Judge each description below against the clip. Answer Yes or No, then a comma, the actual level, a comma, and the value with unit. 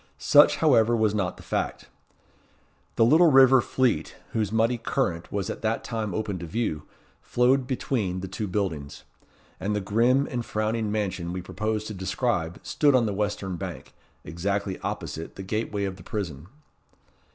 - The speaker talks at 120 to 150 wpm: No, average, 165 wpm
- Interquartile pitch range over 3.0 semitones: Yes, average, 3.8 semitones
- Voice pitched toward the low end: Yes, low, 105 Hz